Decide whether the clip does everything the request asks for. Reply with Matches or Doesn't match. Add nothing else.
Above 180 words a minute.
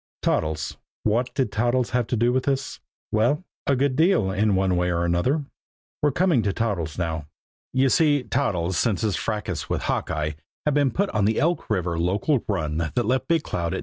Matches